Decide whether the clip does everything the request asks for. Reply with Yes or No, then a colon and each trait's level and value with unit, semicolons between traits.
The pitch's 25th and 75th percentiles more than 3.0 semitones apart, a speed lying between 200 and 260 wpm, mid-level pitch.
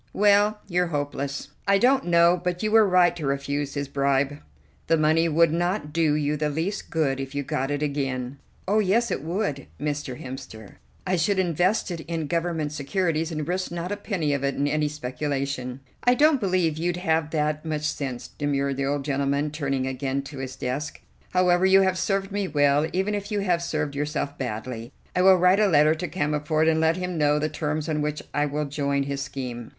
Yes: average, 4.1 semitones; fast, 205 wpm; medium, 150 Hz